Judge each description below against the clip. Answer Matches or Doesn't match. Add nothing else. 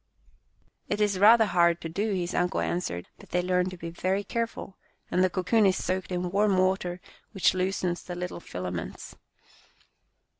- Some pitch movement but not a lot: Doesn't match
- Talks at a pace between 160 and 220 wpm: Matches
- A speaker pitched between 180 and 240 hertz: Matches